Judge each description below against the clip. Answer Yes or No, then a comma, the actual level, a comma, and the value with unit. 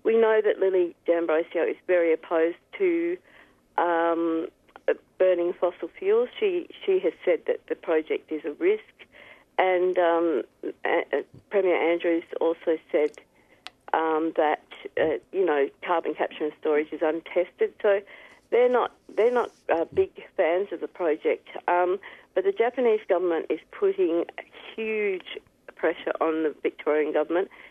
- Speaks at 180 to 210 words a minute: No, average, 145 wpm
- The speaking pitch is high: Yes, high, 195 Hz